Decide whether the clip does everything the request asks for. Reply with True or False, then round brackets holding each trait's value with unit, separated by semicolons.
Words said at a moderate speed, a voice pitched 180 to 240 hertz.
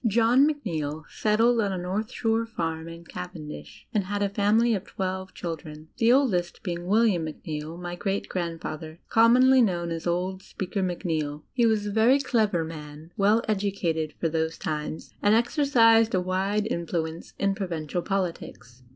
True (160 wpm; 185 Hz)